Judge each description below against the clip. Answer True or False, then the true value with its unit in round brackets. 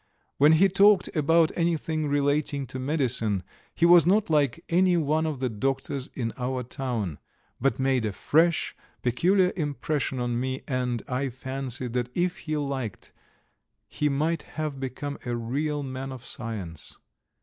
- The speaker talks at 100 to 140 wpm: False (150 wpm)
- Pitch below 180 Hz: True (135 Hz)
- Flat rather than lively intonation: False (3.8 semitones)